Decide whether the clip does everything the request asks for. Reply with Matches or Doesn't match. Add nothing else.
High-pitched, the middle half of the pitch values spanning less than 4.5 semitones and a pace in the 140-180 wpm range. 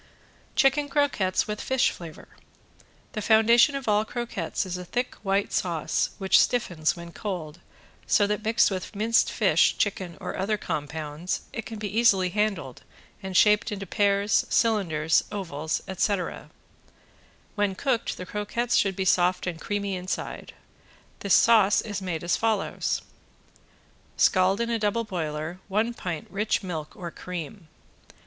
Matches